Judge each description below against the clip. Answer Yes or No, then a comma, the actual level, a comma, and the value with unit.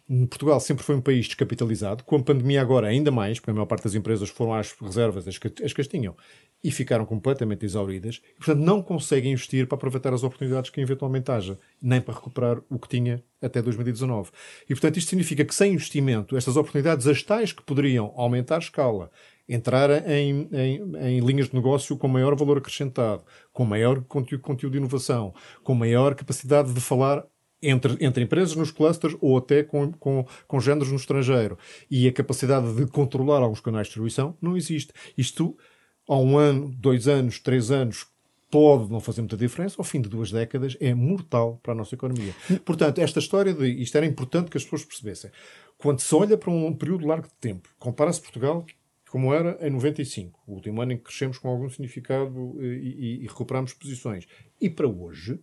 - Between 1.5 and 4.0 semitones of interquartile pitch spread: Yes, average, 3.2 semitones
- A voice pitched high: No, low, 135 Hz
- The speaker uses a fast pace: Yes, fast, 195 wpm